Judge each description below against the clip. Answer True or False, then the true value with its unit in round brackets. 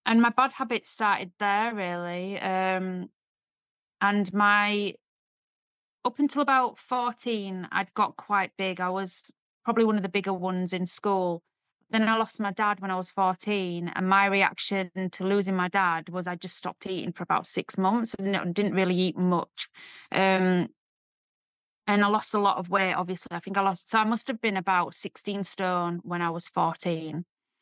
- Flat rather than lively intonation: True (2.1 semitones)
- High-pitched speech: True (195 Hz)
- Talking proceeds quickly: False (180 wpm)